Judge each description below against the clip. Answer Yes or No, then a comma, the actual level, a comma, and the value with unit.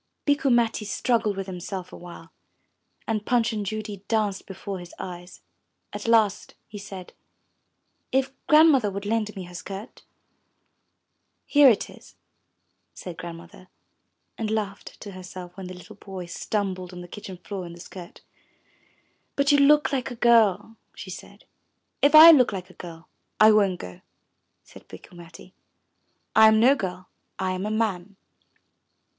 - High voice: Yes, high, 200 Hz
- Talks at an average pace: Yes, average, 155 wpm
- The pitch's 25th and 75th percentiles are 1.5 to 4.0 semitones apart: Yes, average, 3.6 semitones